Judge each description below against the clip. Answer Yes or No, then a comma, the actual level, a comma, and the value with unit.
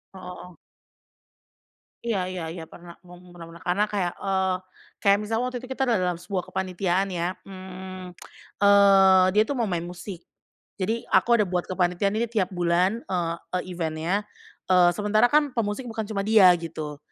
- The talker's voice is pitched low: No, high, 190 Hz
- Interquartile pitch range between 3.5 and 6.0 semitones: No, average, 2.8 semitones